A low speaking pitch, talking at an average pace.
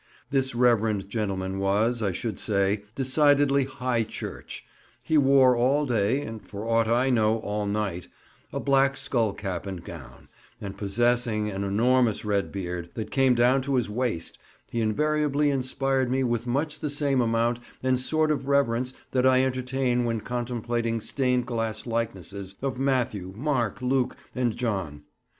Yes: low, 120 Hz; average, 155 wpm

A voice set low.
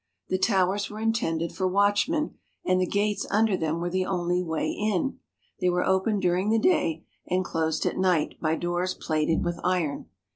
No: medium, 185 Hz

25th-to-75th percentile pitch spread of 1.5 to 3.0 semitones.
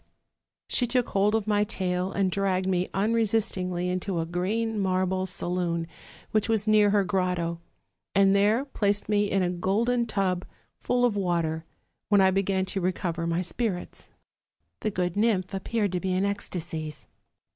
Yes: narrow, 2.5 semitones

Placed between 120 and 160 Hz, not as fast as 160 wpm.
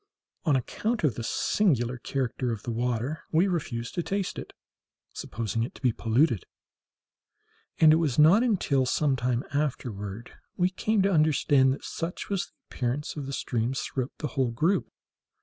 No: low, 135 Hz; average, 165 wpm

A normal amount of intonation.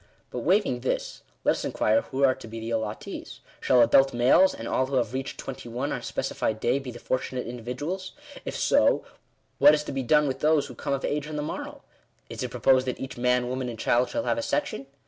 Yes: average, 3.3 semitones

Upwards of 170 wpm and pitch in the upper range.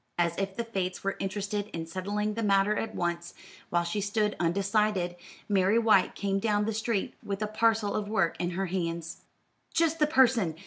Yes: average, 185 wpm; high, 200 Hz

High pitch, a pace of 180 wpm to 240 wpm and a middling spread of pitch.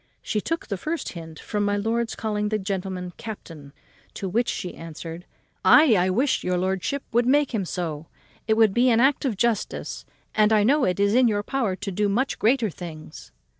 Yes: high, 210 Hz; average, 200 wpm; average, 4.5 semitones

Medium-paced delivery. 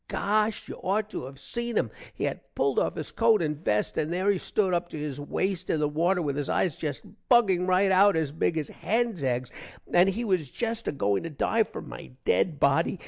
No: fast, 230 wpm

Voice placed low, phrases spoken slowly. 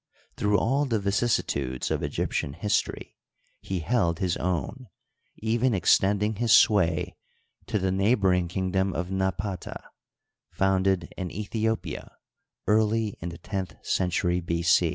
Yes: very low, 95 Hz; slow, 125 wpm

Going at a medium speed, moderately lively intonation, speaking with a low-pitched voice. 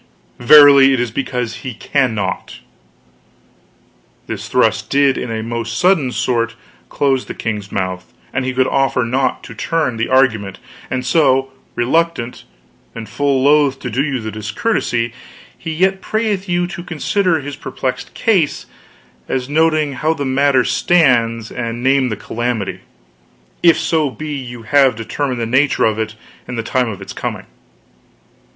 Yes: average, 155 wpm; average, 4.0 semitones; low, 130 Hz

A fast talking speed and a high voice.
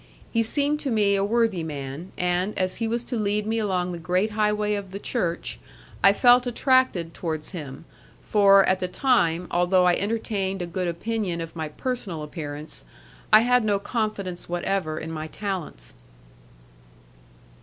No: average, 165 wpm; high, 195 Hz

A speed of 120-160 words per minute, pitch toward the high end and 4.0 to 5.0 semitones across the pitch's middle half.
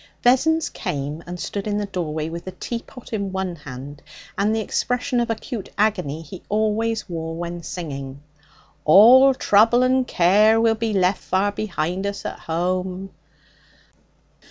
Yes: average, 150 wpm; high, 195 Hz; average, 4.6 semitones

